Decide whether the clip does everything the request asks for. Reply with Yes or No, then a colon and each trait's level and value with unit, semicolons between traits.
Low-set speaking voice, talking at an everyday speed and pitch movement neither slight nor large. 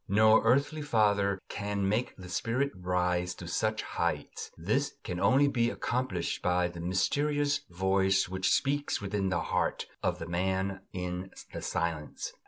Yes: very low, 95 Hz; average, 150 wpm; average, 4.3 semitones